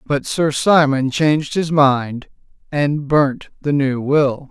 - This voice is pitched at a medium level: Yes, medium, 145 Hz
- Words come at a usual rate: Yes, average, 145 wpm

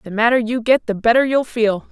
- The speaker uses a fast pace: Yes, fast, 250 wpm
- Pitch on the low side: No, high, 230 Hz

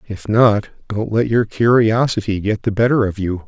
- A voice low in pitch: Yes, low, 110 Hz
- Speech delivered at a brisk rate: No, average, 190 wpm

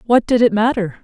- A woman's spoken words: Yes, female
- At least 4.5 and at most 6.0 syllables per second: Yes, 5.4 syllables/s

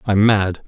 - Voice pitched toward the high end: No, low, 100 Hz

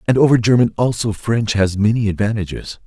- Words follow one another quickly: No, average, 165 wpm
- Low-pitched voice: Yes, low, 110 Hz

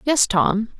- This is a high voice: Yes, high, 215 Hz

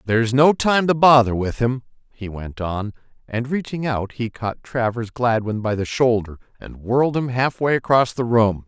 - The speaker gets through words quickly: No, average, 195 wpm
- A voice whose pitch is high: No, low, 120 Hz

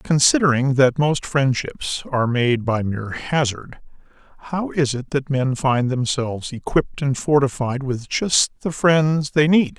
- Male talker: Yes, male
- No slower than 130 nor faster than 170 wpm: Yes, average, 155 wpm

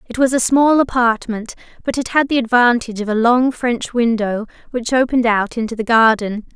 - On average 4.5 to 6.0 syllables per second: Yes, 5.3 syllables/s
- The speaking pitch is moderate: No, high, 235 Hz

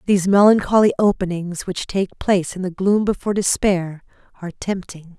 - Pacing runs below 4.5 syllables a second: No, 5.5 syllables/s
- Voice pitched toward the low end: No, high, 190 Hz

